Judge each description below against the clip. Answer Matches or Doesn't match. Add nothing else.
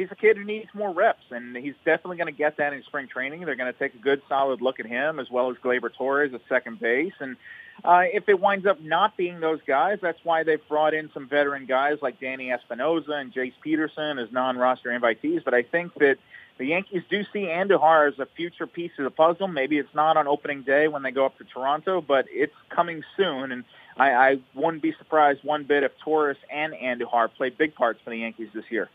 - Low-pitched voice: Doesn't match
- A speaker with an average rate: Doesn't match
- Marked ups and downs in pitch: Doesn't match